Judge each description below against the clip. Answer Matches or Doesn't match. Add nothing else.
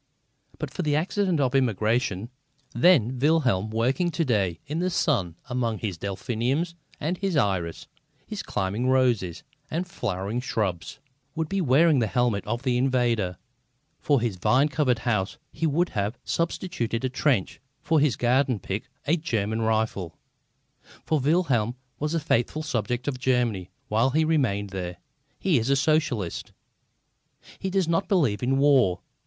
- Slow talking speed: Doesn't match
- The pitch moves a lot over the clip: Matches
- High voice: Doesn't match